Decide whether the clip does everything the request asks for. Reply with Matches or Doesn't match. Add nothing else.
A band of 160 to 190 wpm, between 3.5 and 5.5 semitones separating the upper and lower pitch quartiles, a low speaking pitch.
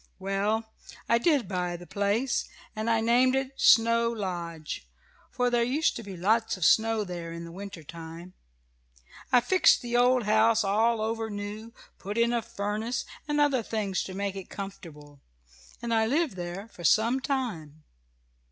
Doesn't match